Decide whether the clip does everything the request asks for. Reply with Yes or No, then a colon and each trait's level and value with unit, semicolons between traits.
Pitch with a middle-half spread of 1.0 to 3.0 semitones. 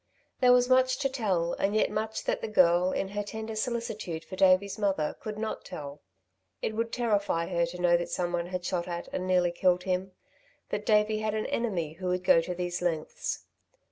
No: average, 3.7 semitones